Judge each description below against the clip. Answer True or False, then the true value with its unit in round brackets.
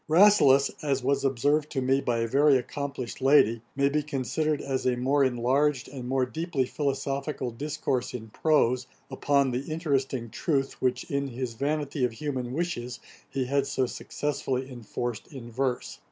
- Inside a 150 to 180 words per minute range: True (160 wpm)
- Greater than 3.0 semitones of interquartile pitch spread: False (2.4 semitones)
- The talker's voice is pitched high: False (135 Hz)